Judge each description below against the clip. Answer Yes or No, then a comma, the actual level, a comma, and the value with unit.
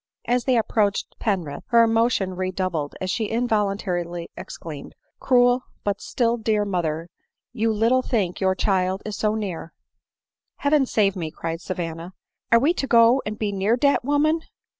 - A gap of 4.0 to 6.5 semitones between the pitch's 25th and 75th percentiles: Yes, average, 4.3 semitones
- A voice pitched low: No, high, 210 Hz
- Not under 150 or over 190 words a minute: Yes, average, 180 wpm